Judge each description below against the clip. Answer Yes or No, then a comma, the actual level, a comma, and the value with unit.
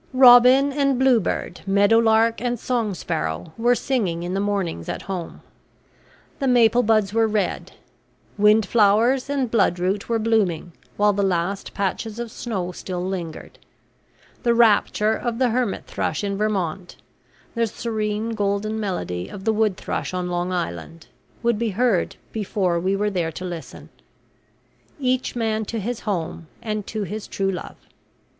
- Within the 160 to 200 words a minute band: No, average, 145 wpm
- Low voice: No, high, 210 Hz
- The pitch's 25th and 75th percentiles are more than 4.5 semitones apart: No, average, 3.8 semitones